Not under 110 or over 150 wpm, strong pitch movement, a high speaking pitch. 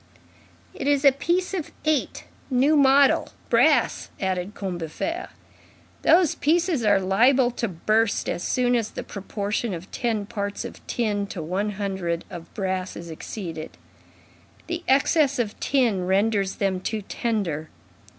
Yes: average, 140 wpm; wide, 6.0 semitones; high, 210 Hz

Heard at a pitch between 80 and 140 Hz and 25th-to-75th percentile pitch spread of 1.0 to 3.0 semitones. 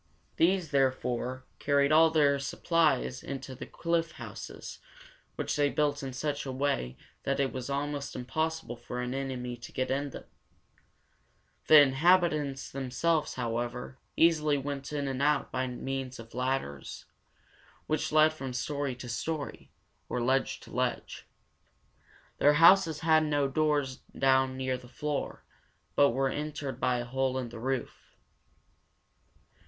Yes: low, 135 Hz; average, 2.7 semitones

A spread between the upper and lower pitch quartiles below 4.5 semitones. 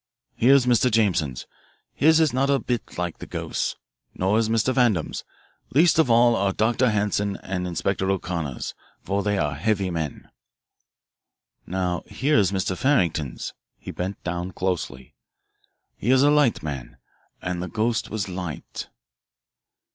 No: average, 5.2 semitones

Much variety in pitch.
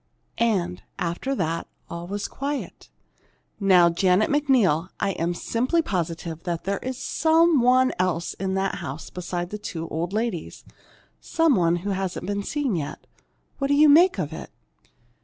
Yes: wide, 7.0 semitones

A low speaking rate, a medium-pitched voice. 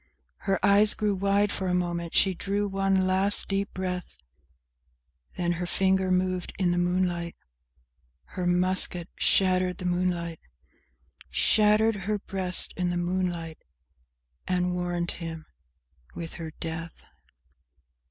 Yes: slow, 120 wpm; medium, 180 Hz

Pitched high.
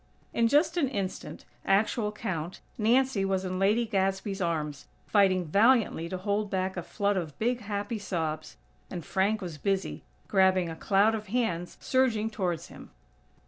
Yes: high, 195 Hz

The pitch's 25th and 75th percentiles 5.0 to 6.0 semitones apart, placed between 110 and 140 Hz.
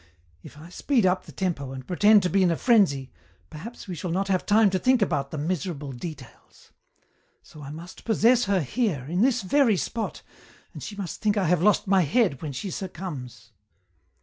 No: wide, 5.4 semitones; medium, 185 Hz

